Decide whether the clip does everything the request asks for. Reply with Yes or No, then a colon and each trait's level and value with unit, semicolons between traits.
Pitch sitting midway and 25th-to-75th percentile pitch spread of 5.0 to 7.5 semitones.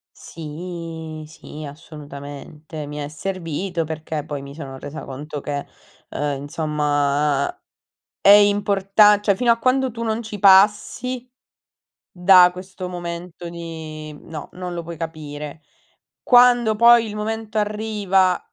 Yes: medium, 170 Hz; wide, 5.5 semitones